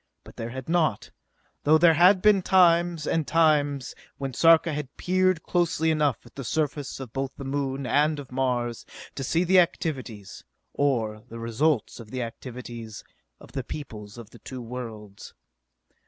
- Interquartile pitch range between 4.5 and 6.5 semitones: Yes, average, 5.1 semitones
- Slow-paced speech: No, average, 165 wpm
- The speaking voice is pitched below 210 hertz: Yes, medium, 140 Hz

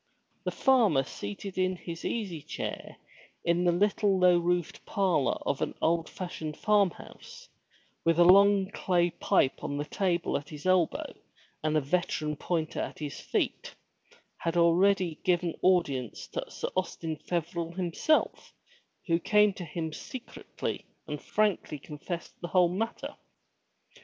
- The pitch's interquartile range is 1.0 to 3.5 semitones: Yes, average, 2.9 semitones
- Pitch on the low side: No, medium, 175 Hz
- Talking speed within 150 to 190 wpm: No, average, 140 wpm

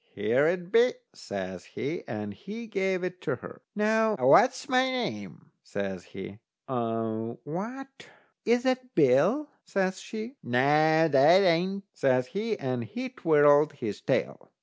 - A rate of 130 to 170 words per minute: Yes, slow, 135 wpm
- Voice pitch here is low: No, medium, 175 Hz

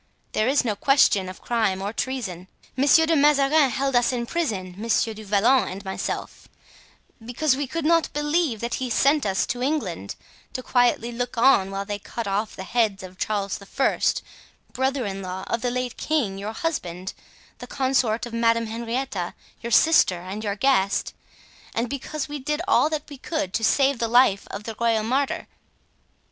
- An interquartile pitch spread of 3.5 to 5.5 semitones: Yes, average, 5.2 semitones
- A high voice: Yes, high, 235 Hz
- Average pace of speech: Yes, average, 185 wpm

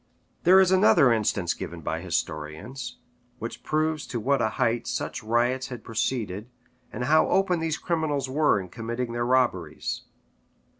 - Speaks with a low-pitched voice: Yes, low, 125 Hz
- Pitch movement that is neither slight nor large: Yes, average, 5.0 semitones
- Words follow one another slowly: No, average, 150 wpm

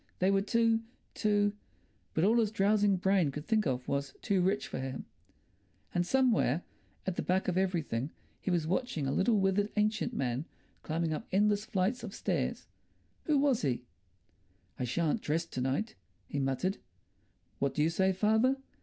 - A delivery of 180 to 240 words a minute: No, average, 165 wpm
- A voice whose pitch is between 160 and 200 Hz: Yes, high, 190 Hz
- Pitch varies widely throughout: Yes, wide, 5.7 semitones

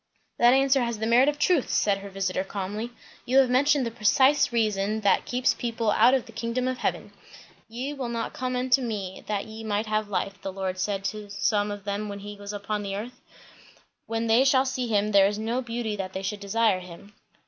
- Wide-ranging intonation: No, average, 3.5 semitones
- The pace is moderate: No, fast, 215 wpm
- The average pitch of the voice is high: Yes, high, 220 Hz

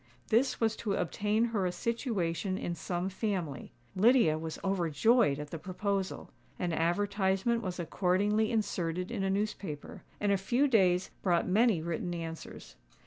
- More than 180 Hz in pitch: Yes, high, 190 Hz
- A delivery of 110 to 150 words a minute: Yes, average, 145 wpm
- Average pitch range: Yes, average, 3.8 semitones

